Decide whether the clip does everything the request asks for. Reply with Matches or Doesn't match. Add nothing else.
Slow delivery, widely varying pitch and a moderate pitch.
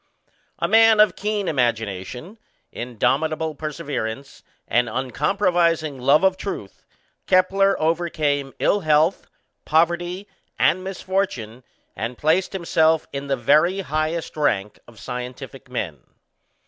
Matches